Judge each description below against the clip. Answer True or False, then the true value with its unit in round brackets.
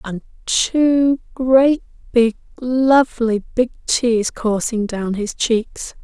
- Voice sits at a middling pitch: False (240 Hz)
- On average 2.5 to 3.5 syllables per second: True (2.9 syllables/s)